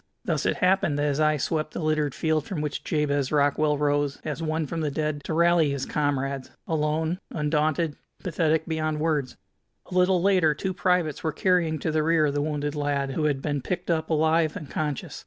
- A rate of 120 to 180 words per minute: No, average, 195 wpm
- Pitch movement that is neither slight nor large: No, narrow, 1.8 semitones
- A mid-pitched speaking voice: Yes, medium, 155 Hz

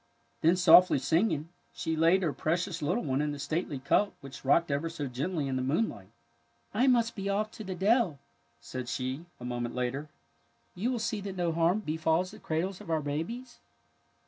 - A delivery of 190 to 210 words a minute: Yes, average, 200 wpm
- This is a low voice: No, medium, 165 Hz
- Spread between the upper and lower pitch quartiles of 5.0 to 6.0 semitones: Yes, wide, 5.5 semitones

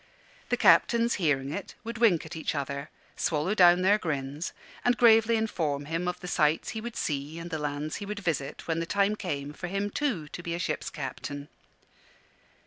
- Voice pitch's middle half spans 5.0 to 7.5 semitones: Yes, wide, 5.6 semitones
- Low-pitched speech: No, medium, 170 Hz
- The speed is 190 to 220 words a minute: Yes, average, 195 wpm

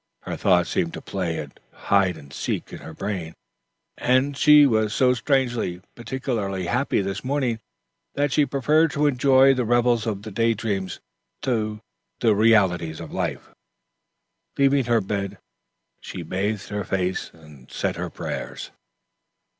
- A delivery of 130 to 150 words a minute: Yes, average, 145 wpm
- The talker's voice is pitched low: Yes, low, 110 Hz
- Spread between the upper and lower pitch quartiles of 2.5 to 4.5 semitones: No, wide, 5.6 semitones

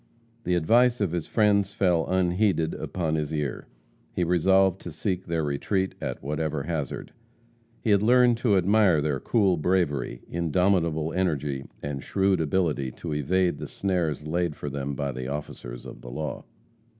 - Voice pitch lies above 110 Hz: No, very low, 85 Hz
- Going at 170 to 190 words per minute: No, average, 160 wpm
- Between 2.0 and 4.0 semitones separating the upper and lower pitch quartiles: No, average, 4.4 semitones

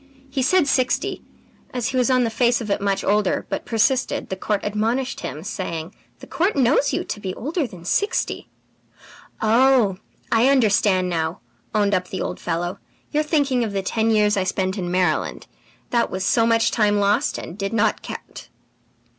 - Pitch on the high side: Yes, high, 215 Hz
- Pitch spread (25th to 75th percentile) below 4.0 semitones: No, average, 4.8 semitones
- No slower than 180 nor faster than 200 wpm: Yes, average, 185 wpm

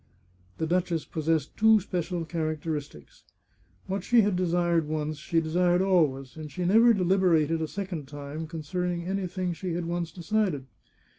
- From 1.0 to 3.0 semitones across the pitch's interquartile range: Yes, average, 2.7 semitones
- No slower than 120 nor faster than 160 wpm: Yes, average, 150 wpm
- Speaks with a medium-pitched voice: Yes, medium, 170 Hz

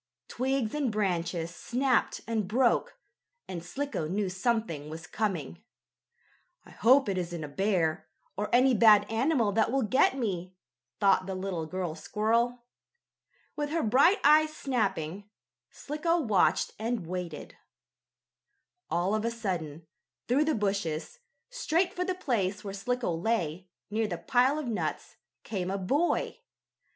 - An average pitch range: No, wide, 5.9 semitones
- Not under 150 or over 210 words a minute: No, average, 140 wpm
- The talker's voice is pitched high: Yes, high, 215 Hz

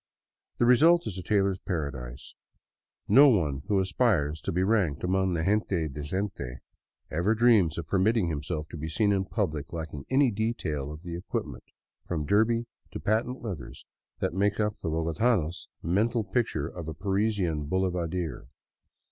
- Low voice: Yes, very low, 95 Hz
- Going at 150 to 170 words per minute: Yes, average, 155 wpm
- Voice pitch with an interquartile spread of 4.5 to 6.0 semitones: Yes, average, 5.3 semitones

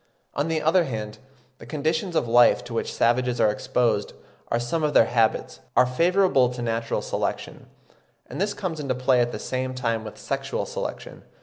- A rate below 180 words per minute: No, average, 185 wpm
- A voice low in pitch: Yes, low, 125 Hz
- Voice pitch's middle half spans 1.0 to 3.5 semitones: No, average, 4.9 semitones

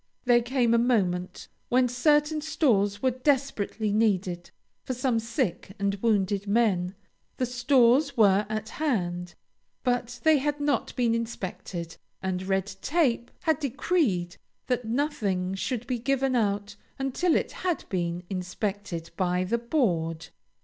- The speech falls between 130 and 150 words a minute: Yes, slow, 135 wpm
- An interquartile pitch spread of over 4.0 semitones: Yes, average, 5.2 semitones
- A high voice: Yes, high, 230 Hz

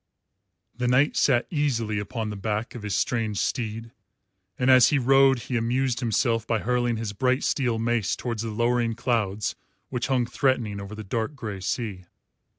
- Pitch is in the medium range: No, low, 115 Hz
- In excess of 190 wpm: No, average, 170 wpm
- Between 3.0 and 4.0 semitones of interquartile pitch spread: No, narrow, 2.6 semitones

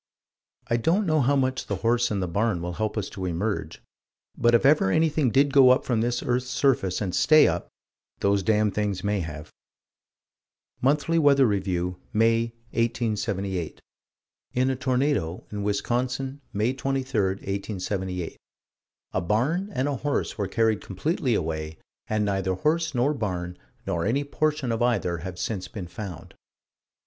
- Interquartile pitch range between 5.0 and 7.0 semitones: Yes, wide, 5.5 semitones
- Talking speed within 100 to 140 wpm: No, average, 155 wpm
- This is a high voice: No, low, 110 Hz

